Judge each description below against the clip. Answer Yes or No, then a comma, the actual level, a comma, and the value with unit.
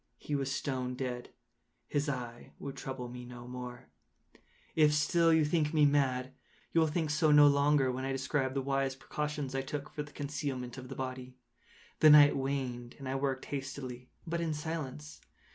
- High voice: No, low, 135 Hz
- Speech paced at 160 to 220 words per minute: Yes, average, 180 wpm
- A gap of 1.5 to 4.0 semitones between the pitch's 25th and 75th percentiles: Yes, narrow, 2.6 semitones